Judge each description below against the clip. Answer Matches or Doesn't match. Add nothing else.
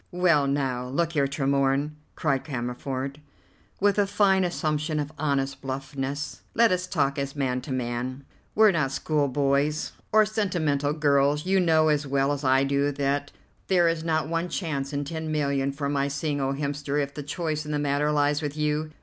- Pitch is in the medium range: Matches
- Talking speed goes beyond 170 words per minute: Matches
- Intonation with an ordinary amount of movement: Doesn't match